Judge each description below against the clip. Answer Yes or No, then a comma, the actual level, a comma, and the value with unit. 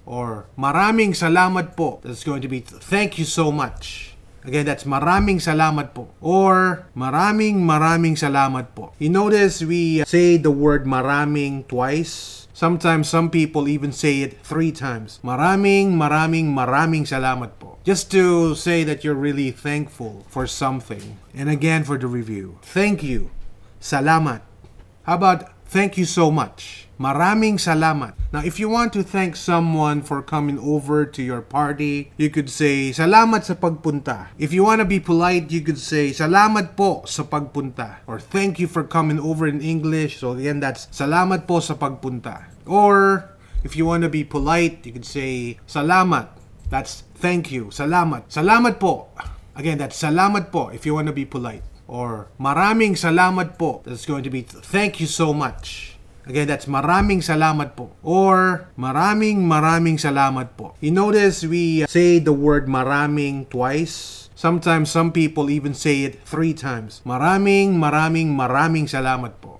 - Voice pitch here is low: No, medium, 150 Hz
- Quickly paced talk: Yes, fast, 160 wpm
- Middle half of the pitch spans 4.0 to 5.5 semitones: Yes, average, 4.6 semitones